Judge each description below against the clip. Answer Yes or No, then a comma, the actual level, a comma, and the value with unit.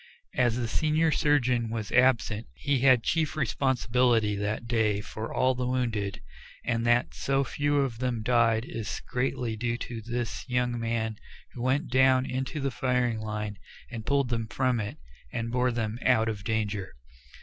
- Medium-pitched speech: No, low, 120 Hz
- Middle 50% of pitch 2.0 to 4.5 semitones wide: Yes, narrow, 2.4 semitones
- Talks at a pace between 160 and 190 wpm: Yes, average, 165 wpm